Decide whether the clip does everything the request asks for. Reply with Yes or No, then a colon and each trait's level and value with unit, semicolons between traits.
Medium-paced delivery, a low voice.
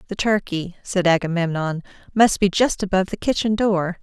No: average, 165 wpm; high, 190 Hz